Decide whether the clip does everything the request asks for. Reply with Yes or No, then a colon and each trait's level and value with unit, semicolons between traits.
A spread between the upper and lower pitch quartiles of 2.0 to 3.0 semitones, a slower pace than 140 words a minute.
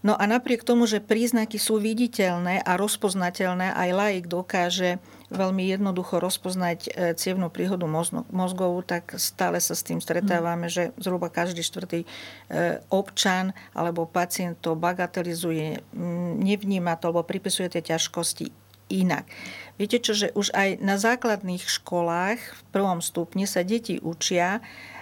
Yes: narrow, 2.6 semitones; average, 130 wpm